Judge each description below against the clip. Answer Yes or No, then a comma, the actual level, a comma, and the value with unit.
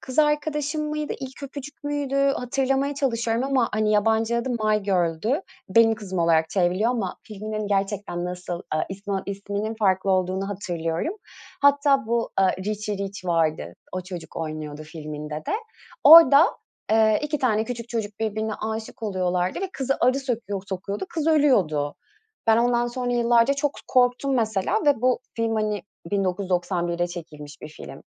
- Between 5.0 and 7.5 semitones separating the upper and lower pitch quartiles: Yes, wide, 5.6 semitones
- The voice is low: No, high, 215 Hz